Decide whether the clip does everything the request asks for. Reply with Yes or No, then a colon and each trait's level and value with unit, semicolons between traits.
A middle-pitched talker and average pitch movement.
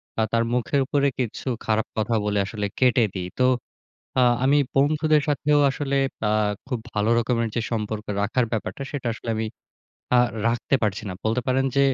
No: low, 120 Hz; average, 3.9 semitones